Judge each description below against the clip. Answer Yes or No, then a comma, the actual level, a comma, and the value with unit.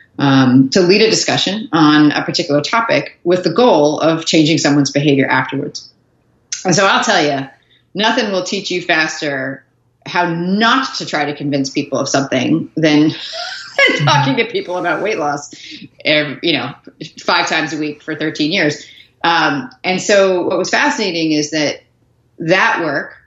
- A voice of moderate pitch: Yes, medium, 155 Hz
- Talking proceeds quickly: No, average, 160 wpm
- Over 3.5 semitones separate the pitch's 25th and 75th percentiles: Yes, average, 4.0 semitones